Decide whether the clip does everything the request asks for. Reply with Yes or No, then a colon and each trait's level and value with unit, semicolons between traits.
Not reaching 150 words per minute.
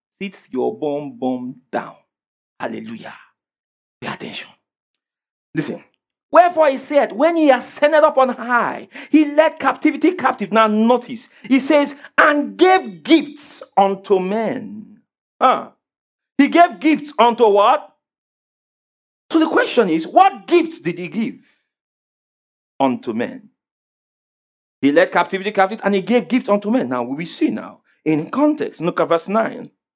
Yes: slow, 135 wpm